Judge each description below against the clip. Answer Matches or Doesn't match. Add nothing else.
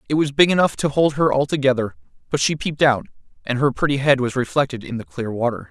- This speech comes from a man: Matches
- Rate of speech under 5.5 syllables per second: Doesn't match